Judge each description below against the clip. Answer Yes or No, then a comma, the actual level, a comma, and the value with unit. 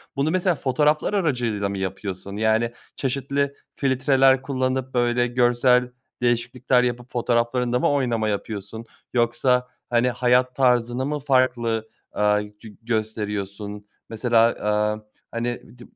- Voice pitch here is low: Yes, low, 120 Hz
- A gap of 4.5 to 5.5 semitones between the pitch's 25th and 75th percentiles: No, average, 2.8 semitones